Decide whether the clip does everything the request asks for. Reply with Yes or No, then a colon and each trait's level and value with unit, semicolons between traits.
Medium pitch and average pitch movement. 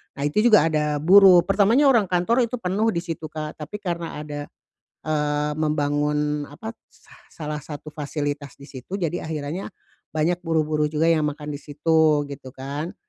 Yes: medium, 155 Hz; average, 3.1 semitones